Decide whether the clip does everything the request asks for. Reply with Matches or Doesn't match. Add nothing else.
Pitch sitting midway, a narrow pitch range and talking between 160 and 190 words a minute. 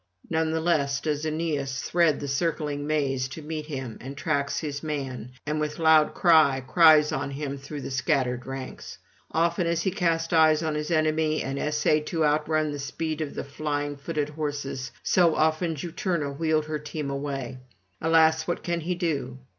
Matches